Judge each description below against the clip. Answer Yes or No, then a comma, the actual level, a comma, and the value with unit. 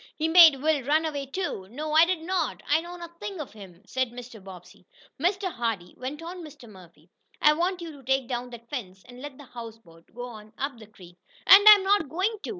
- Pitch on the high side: Yes, very high, 275 Hz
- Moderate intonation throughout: No, wide, 6.7 semitones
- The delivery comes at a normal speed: No, fast, 220 wpm